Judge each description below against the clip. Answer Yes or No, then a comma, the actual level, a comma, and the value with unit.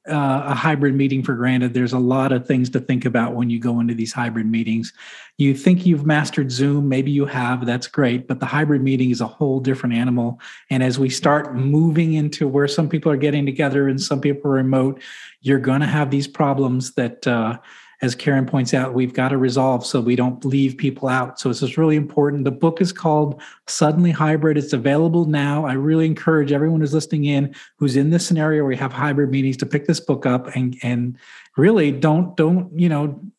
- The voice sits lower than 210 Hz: Yes, medium, 140 Hz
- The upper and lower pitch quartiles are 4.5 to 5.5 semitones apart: No, average, 2.7 semitones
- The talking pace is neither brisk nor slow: No, fast, 215 wpm